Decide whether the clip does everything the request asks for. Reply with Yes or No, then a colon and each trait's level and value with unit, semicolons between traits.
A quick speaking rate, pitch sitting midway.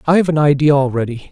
No: average, 185 wpm; medium, 145 Hz